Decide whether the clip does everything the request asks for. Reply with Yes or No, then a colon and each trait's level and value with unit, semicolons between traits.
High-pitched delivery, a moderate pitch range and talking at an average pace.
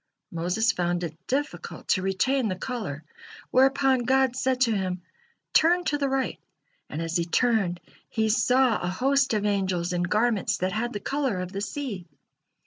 No: high, 215 Hz; wide, 6.3 semitones; average, 170 wpm